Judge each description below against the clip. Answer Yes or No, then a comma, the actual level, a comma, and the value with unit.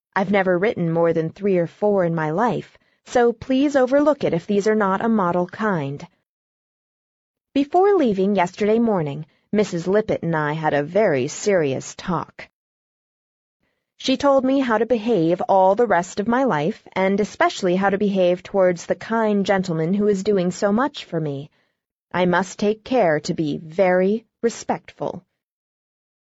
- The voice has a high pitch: Yes, high, 200 Hz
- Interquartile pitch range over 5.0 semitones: No, average, 4.3 semitones